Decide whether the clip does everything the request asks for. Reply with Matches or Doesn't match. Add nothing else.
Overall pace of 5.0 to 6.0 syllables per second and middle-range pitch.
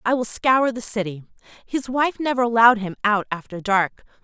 Doesn't match